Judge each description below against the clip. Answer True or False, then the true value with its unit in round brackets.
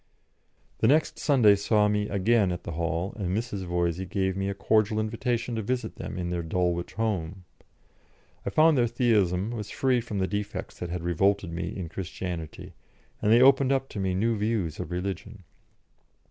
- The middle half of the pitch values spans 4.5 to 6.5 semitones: False (4.0 semitones)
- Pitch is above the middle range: False (100 Hz)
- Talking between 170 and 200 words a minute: True (180 wpm)